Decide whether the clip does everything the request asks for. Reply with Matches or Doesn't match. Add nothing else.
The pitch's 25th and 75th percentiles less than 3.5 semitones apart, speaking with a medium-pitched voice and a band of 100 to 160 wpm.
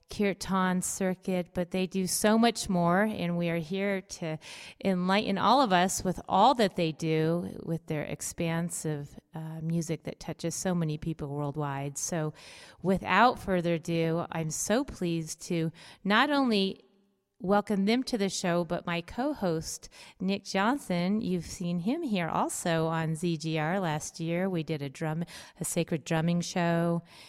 Matches